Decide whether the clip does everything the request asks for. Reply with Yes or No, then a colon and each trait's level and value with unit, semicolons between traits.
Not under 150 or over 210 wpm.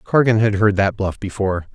Yes: fast, 205 wpm